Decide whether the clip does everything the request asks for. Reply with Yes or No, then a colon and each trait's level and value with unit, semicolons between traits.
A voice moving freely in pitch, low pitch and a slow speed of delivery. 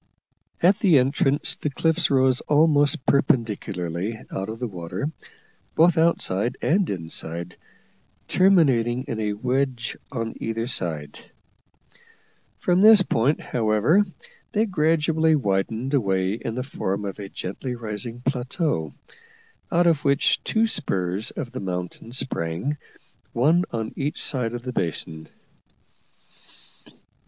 Yes: wide, 6.8 semitones; low, 125 Hz; slow, 120 wpm